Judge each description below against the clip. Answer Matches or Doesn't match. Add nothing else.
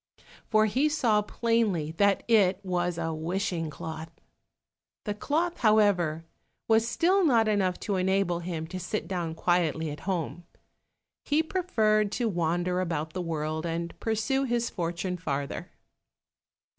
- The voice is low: Doesn't match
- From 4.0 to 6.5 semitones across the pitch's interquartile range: Matches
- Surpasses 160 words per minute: Doesn't match